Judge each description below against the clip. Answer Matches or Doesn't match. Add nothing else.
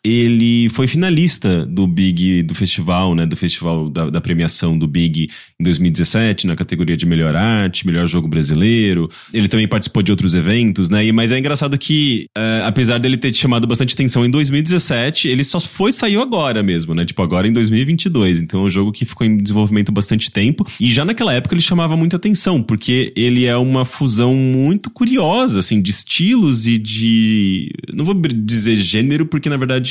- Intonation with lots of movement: Matches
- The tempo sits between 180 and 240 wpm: Matches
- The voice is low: Matches